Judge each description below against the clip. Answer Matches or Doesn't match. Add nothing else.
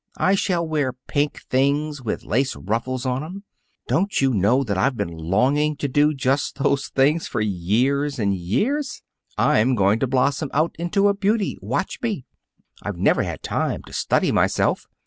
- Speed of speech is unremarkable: Matches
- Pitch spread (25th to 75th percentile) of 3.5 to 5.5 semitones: Matches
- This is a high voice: Doesn't match